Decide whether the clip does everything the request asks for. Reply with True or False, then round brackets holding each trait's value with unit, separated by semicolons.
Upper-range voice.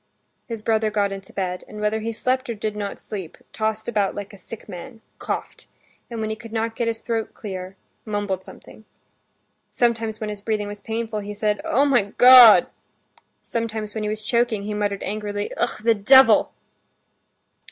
True (215 Hz)